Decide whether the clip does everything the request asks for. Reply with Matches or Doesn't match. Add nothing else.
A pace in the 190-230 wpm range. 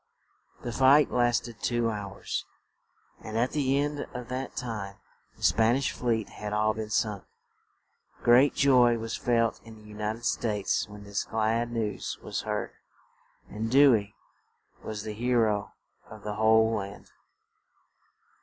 Doesn't match